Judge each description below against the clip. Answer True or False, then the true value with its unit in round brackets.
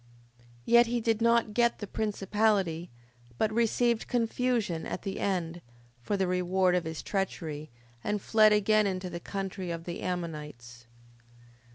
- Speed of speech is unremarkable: True (150 wpm)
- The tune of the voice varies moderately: True (4.2 semitones)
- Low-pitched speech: False (195 Hz)